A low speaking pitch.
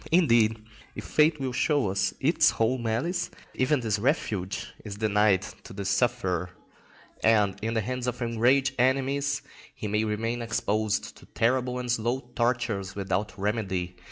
Yes: low, 115 Hz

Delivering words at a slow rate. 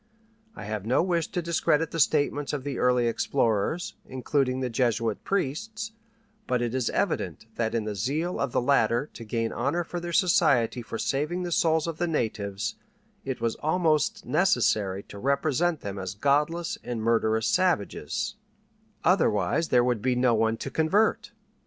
No: average, 165 wpm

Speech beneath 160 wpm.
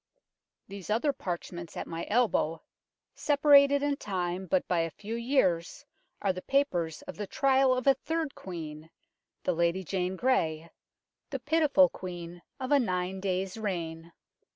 Yes: average, 150 wpm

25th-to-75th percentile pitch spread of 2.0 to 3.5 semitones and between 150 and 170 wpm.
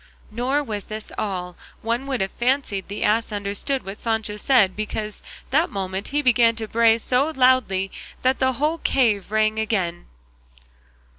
No: average, 4.1 semitones; average, 155 wpm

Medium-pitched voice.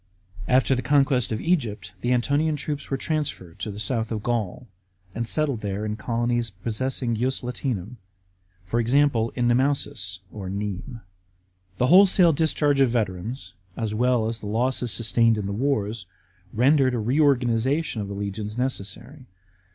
No: low, 120 Hz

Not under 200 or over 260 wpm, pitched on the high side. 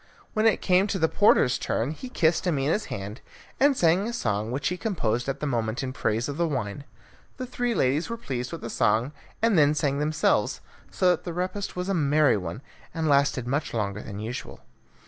No: fast, 205 wpm; medium, 145 Hz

